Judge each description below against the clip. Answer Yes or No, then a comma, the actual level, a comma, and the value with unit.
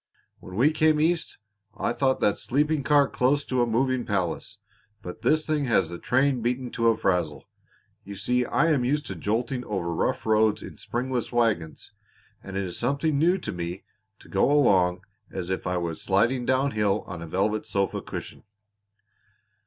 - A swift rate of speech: No, average, 180 wpm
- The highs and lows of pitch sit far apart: Yes, wide, 6.0 semitones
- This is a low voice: Yes, low, 115 Hz